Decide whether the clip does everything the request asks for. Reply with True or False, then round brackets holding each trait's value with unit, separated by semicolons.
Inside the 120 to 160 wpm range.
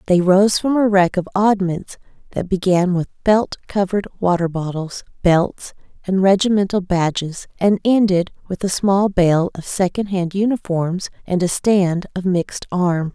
True (150 wpm)